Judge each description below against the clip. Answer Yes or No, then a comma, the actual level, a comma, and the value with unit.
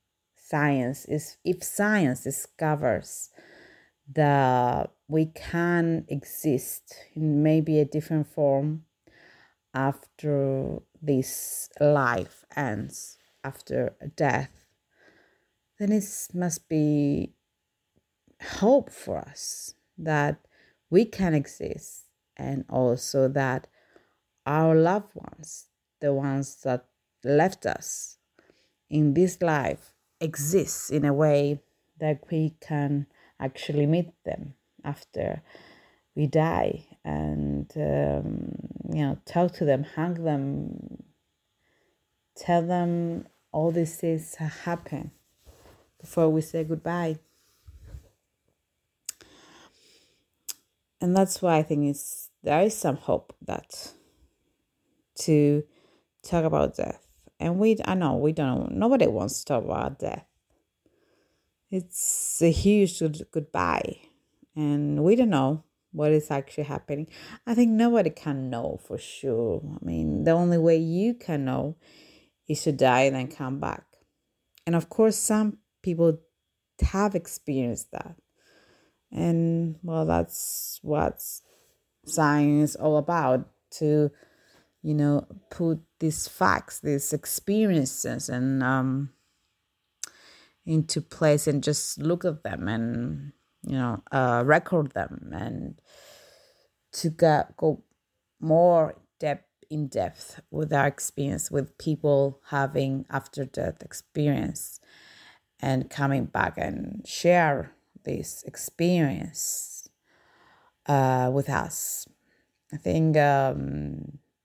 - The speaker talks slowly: Yes, slow, 110 wpm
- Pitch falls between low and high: Yes, medium, 150 Hz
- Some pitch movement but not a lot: Yes, average, 3.4 semitones